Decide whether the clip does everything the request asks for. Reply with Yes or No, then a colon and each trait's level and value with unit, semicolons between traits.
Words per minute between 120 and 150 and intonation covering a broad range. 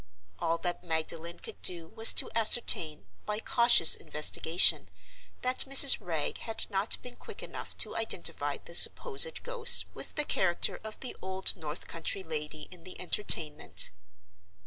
Yes: average, 145 wpm; wide, 6.6 semitones